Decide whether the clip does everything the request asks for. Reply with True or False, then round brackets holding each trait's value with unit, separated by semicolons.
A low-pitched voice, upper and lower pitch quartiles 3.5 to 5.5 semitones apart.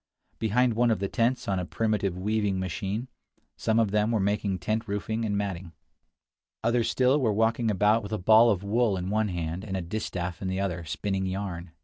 False (105 Hz; 3.0 semitones)